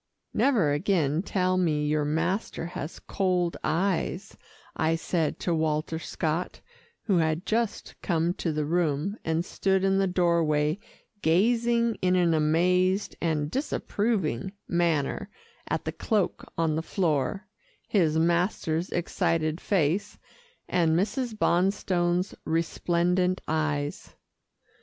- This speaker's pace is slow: Yes, slow, 115 wpm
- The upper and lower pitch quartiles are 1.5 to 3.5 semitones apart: Yes, average, 3.2 semitones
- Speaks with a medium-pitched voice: Yes, medium, 175 Hz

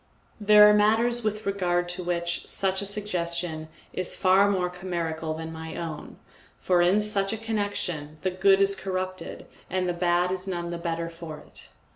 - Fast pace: No, average, 175 wpm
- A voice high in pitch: No, medium, 180 Hz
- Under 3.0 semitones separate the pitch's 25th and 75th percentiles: Yes, narrow, 2.6 semitones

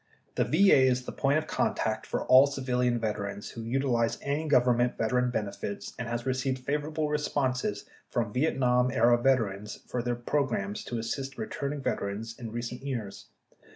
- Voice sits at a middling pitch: No, low, 125 Hz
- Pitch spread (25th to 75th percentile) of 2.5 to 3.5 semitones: Yes, average, 2.9 semitones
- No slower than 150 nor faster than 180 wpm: Yes, average, 155 wpm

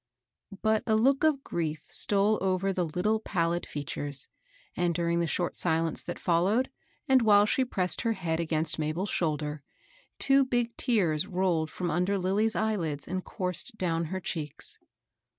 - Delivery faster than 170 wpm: No, average, 155 wpm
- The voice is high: No, medium, 180 Hz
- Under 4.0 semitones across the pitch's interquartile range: No, average, 4.7 semitones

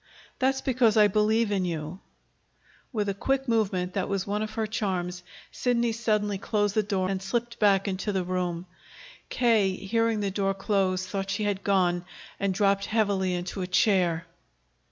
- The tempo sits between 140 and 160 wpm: No, average, 170 wpm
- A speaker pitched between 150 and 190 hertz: No, high, 200 Hz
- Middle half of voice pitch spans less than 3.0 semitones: Yes, narrow, 2.5 semitones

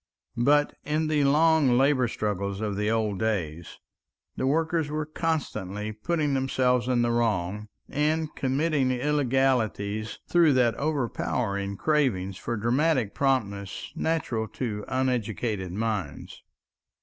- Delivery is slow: Yes, slow, 115 wpm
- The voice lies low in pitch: Yes, low, 125 Hz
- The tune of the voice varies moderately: No, wide, 5.8 semitones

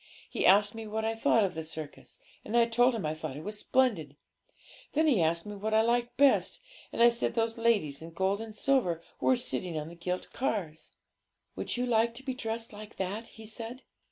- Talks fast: Yes, fast, 215 wpm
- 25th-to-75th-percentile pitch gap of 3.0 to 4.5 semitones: No, average, 5.1 semitones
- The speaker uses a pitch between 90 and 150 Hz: No, high, 220 Hz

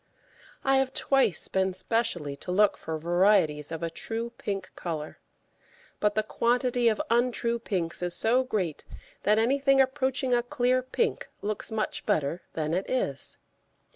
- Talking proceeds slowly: No, average, 150 wpm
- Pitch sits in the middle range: No, high, 215 Hz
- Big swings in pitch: Yes, wide, 6.0 semitones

